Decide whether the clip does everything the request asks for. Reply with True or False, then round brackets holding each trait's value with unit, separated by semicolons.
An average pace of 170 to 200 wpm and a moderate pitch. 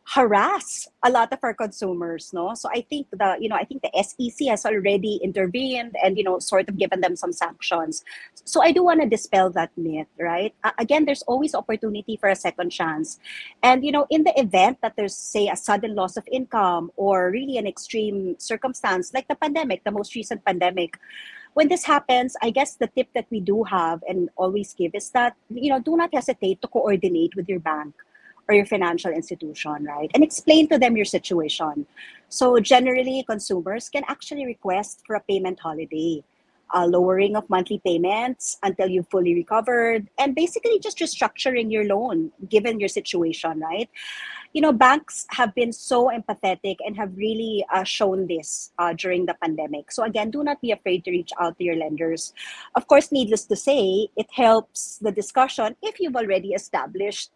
False (190 wpm; 215 Hz)